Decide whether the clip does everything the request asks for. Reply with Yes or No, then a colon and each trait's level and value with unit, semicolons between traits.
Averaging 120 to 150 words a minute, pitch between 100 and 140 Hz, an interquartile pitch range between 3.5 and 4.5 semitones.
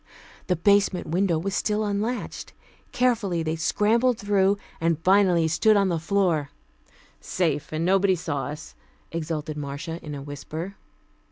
No: average, 140 wpm; medium, 175 Hz; average, 4.1 semitones